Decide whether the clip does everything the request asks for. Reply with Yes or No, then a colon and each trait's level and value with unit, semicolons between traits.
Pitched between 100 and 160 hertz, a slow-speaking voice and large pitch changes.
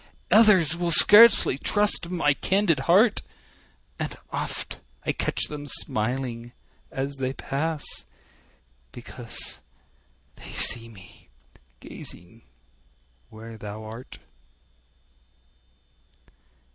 Yes: medium, 140 Hz; slow, 85 wpm; wide, 7.0 semitones